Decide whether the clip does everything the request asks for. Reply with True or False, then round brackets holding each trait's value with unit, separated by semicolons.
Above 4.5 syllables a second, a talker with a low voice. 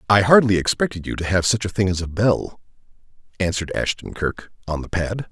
True (5.7 syllables/s; 100 Hz)